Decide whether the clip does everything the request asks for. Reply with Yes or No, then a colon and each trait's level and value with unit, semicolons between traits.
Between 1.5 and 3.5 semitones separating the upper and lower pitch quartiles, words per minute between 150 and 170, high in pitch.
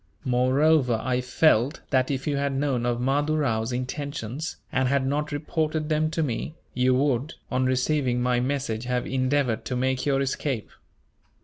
No: narrow, 2.6 semitones; average, 165 wpm; low, 130 Hz